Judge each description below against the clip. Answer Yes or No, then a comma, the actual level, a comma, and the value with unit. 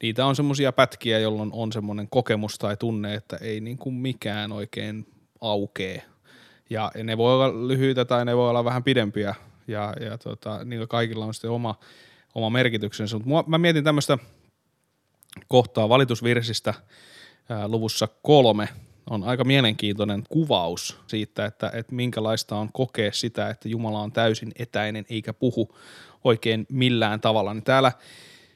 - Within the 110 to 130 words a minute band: No, average, 145 wpm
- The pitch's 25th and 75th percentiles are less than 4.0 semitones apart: Yes, average, 2.7 semitones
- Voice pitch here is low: Yes, low, 115 Hz